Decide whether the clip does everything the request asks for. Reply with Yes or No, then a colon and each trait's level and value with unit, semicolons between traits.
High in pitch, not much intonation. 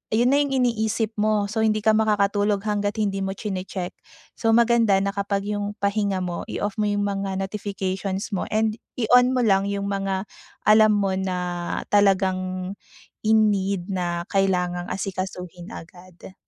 Yes: high, 200 Hz; narrow, 2.1 semitones